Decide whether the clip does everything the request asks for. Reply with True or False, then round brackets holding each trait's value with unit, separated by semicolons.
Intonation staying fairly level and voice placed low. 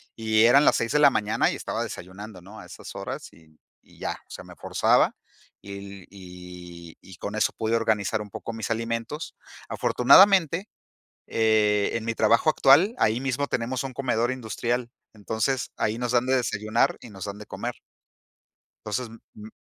False (3.3 semitones; 110 Hz)